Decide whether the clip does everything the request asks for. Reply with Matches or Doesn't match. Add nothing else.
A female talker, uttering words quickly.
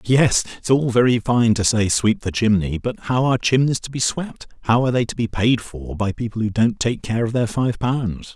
Doesn't match